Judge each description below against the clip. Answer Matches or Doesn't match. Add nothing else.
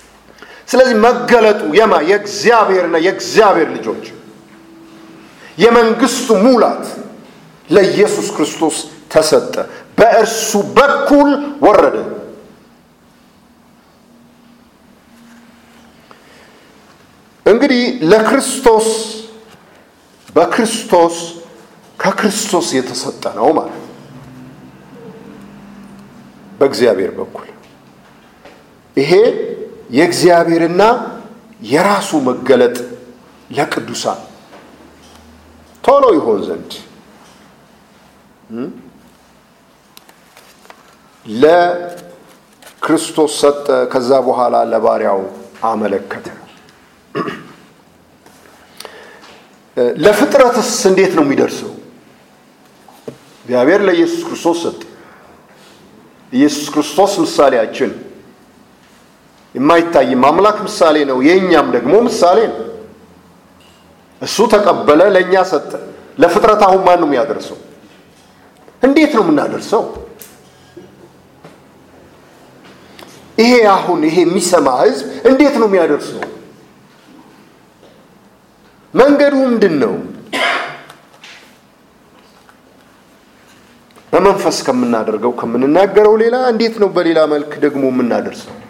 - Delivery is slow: Matches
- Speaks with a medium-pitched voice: Doesn't match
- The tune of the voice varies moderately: Doesn't match